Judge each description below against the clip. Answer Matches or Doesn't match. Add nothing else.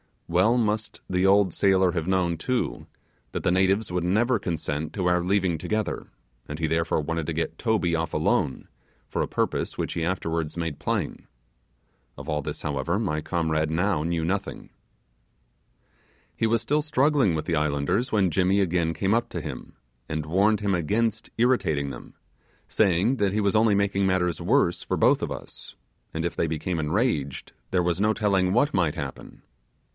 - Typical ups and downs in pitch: Matches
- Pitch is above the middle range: Doesn't match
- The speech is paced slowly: Doesn't match